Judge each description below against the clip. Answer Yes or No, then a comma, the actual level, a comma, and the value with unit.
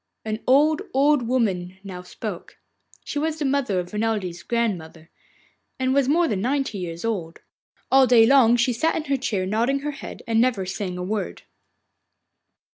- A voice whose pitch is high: Yes, high, 230 Hz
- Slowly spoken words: No, average, 170 wpm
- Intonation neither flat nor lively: No, wide, 6.2 semitones